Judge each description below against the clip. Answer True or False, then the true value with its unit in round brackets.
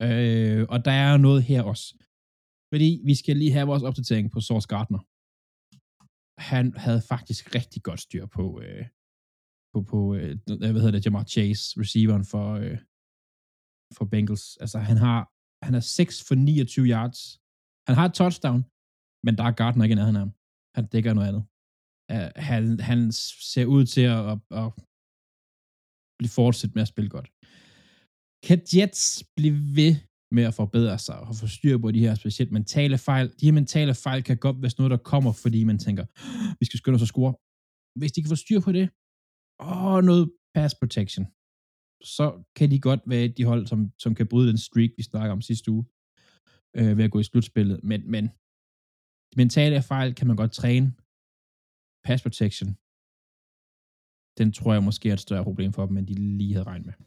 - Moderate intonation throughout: True (4.0 semitones)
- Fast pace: False (185 wpm)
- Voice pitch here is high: False (115 Hz)